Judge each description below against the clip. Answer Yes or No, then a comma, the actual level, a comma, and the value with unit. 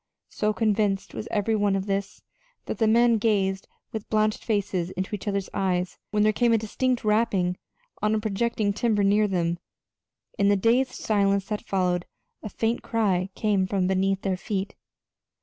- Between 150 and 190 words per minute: Yes, average, 170 wpm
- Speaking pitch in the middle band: No, high, 205 Hz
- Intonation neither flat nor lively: No, narrow, 2.2 semitones